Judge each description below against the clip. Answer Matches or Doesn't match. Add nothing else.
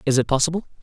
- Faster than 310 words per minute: Doesn't match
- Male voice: Matches